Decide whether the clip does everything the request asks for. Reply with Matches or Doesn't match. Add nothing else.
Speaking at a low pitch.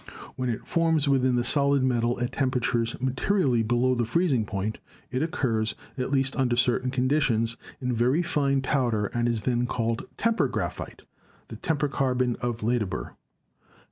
Matches